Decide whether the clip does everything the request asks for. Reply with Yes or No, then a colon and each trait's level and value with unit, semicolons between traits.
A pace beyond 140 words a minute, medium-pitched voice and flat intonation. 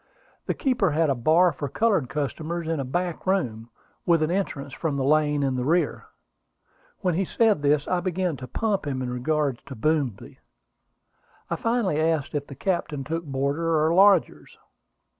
No: average, 175 wpm; medium, 155 Hz; average, 4.2 semitones